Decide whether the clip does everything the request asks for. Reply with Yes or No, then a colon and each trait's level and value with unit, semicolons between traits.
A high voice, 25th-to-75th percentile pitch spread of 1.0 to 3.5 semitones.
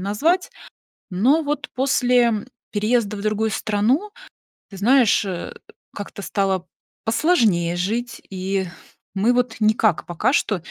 No: high, 215 Hz; average, 4.2 semitones